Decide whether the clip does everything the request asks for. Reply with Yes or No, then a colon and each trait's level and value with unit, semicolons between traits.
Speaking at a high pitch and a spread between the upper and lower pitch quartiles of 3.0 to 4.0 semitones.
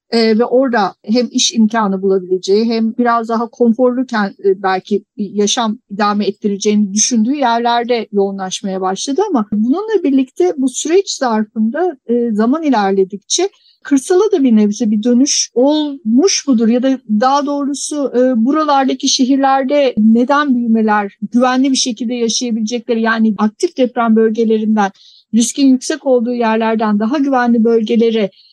Yes: high, 235 Hz; average, 3.7 semitones